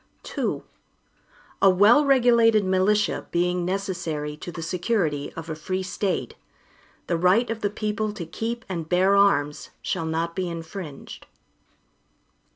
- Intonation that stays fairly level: No, average, 4.1 semitones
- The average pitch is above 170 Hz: Yes, medium, 185 Hz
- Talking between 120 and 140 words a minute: Yes, slow, 135 wpm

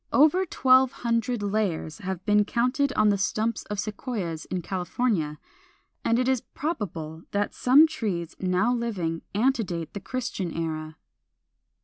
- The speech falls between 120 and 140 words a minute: Yes, slow, 135 wpm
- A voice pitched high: Yes, high, 210 Hz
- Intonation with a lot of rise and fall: Yes, wide, 5.8 semitones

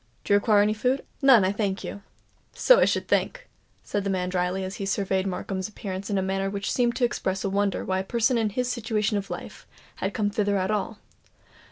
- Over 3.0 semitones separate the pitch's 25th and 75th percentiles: No, narrow, 2.5 semitones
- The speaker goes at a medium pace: No, fast, 225 wpm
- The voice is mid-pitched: No, high, 200 Hz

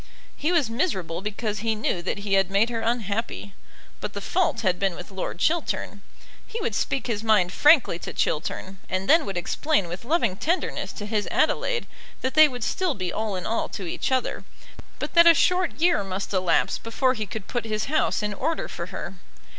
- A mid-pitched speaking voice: No, high, 220 Hz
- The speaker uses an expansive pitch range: Yes, wide, 6.4 semitones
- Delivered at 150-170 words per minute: No, average, 200 wpm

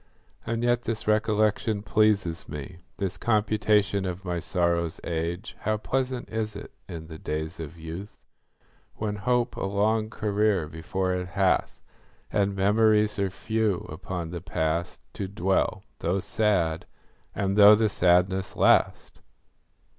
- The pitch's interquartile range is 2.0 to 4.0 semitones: Yes, average, 3.6 semitones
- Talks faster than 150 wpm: No, slow, 135 wpm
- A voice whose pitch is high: No, low, 100 Hz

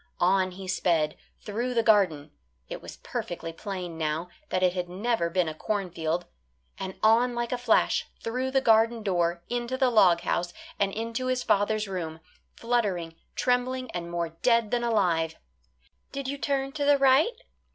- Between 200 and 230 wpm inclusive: No, average, 165 wpm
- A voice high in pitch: Yes, high, 205 Hz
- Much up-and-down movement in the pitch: Yes, wide, 5.8 semitones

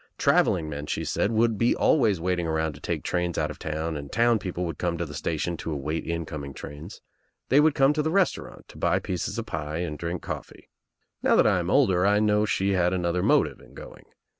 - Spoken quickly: Yes, fast, 225 wpm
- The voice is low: Yes, very low, 90 Hz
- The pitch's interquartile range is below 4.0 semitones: No, average, 4.7 semitones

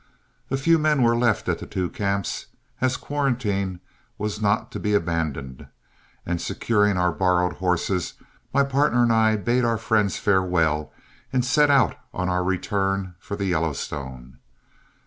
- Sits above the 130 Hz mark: No, low, 100 Hz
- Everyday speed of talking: Yes, average, 150 wpm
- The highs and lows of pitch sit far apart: No, average, 4.9 semitones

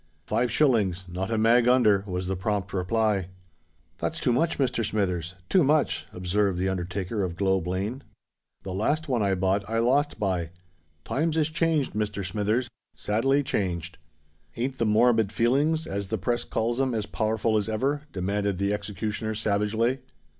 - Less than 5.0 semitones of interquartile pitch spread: Yes, average, 4.3 semitones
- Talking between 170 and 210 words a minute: No, average, 155 wpm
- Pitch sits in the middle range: No, low, 105 Hz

